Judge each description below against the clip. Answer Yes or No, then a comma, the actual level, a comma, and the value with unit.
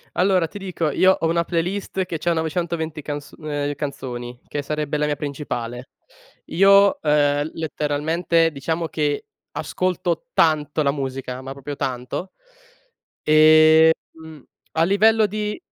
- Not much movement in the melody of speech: No, average, 3.0 semitones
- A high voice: No, medium, 155 Hz